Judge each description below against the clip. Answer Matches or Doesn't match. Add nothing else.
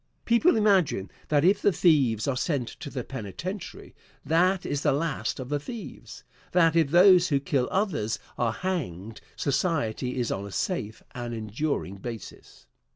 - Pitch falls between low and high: Matches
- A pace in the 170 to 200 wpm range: Doesn't match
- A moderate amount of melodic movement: Doesn't match